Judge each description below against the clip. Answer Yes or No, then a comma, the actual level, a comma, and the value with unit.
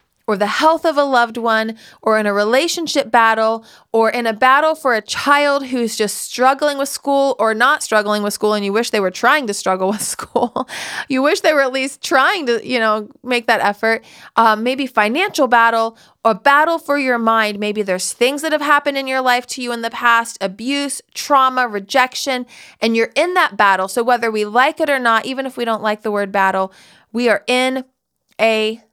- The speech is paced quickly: Yes, fast, 210 wpm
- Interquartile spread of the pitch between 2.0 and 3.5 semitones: No, average, 3.9 semitones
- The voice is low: No, high, 240 Hz